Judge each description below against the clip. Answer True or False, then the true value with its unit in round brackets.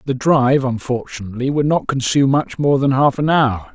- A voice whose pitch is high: False (135 Hz)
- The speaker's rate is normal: True (190 wpm)